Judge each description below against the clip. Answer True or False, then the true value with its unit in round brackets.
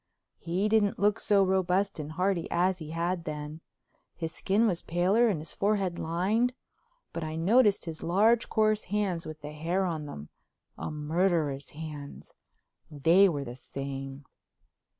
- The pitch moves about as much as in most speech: True (4.3 semitones)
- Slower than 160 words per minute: True (145 wpm)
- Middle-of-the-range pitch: True (170 Hz)